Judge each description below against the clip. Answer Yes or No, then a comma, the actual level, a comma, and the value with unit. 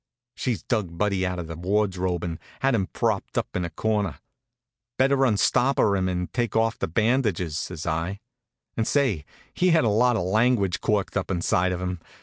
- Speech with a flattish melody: No, average, 4.3 semitones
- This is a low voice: Yes, low, 100 Hz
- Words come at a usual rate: Yes, average, 185 wpm